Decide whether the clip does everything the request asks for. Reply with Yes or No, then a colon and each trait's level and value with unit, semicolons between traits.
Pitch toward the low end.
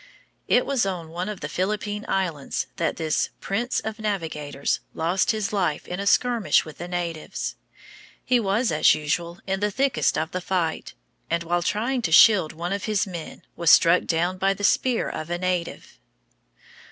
No: medium, 185 Hz